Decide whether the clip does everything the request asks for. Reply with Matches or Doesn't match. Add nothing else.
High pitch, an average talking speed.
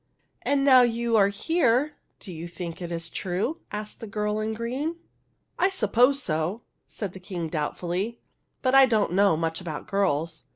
Matches